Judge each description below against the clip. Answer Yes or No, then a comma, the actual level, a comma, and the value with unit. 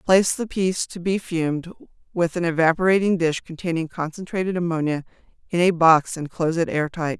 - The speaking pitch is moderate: Yes, medium, 170 Hz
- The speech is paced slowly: No, average, 165 wpm